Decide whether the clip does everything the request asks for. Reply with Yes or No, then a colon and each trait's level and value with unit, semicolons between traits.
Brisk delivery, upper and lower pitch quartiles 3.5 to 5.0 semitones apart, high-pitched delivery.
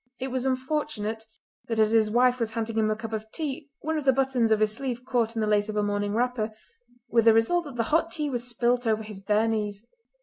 No: fast, 245 wpm; average, 3.1 semitones; high, 230 Hz